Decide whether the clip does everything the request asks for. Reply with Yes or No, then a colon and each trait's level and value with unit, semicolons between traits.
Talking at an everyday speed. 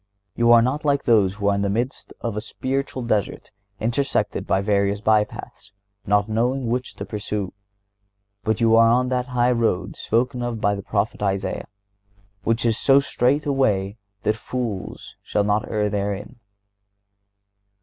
Yes: average, 165 wpm